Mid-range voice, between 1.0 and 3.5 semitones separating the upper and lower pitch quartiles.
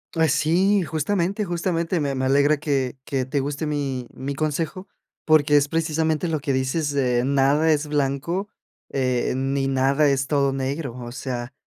Yes: medium, 145 Hz; average, 3.0 semitones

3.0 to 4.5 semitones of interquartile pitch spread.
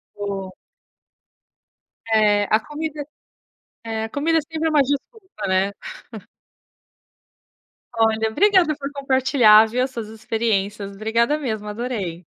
No: average, 5.2 semitones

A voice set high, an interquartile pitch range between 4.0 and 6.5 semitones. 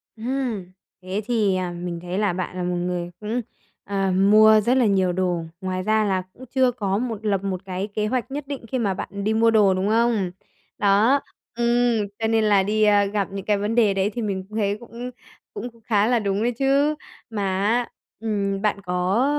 No: high, 210 Hz; average, 3.3 semitones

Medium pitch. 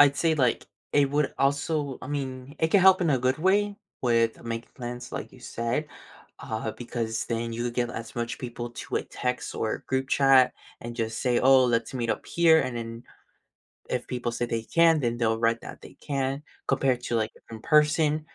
No: low, 125 Hz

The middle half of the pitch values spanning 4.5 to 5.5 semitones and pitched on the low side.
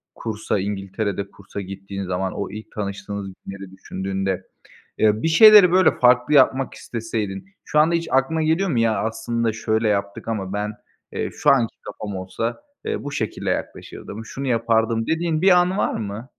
Yes: average, 5.2 semitones; low, 110 Hz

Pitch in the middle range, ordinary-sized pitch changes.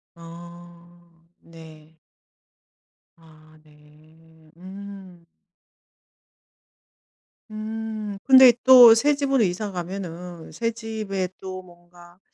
Yes: medium, 180 Hz; average, 4.1 semitones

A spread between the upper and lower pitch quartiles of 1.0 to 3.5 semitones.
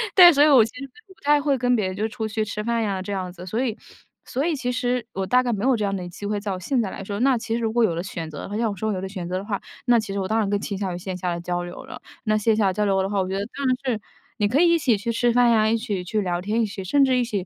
No: average, 4.1 semitones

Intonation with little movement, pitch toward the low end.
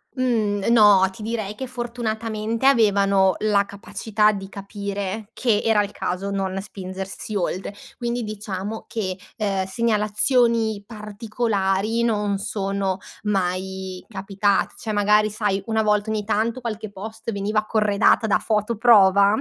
No: narrow, 2.0 semitones; high, 210 Hz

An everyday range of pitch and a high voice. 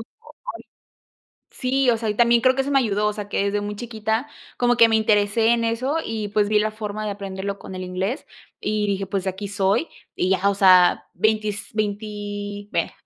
No: narrow, 2.1 semitones; high, 210 Hz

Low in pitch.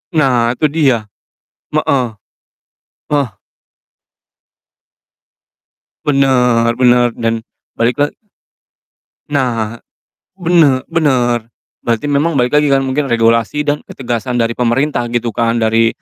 Yes: low, 125 Hz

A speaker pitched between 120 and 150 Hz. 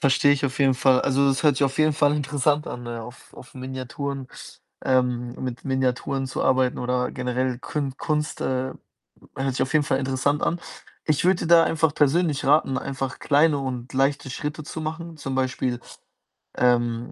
Yes: low, 135 Hz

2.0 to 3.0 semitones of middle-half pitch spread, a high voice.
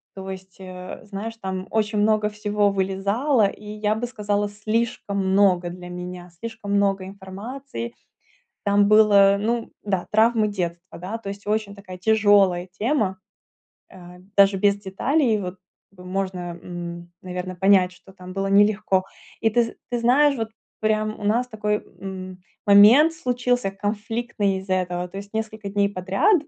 Yes: narrow, 2.5 semitones; high, 200 Hz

